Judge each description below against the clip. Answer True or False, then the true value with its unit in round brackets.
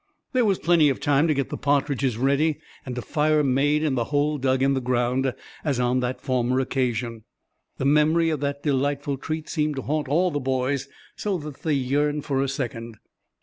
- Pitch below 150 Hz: True (140 Hz)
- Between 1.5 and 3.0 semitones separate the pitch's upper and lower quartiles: True (2.6 semitones)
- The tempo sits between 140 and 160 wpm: False (200 wpm)